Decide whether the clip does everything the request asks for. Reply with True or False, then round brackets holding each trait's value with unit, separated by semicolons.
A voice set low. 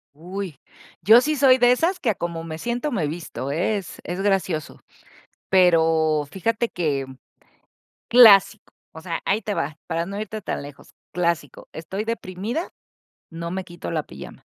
False (185 Hz)